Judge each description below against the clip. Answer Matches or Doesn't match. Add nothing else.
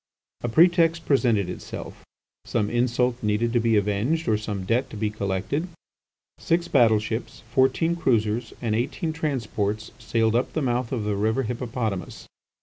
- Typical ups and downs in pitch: Matches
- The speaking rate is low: Doesn't match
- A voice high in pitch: Doesn't match